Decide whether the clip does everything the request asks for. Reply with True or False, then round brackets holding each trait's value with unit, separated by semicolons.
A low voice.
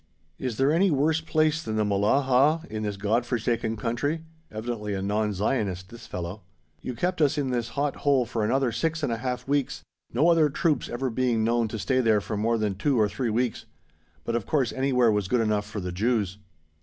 True (120 Hz)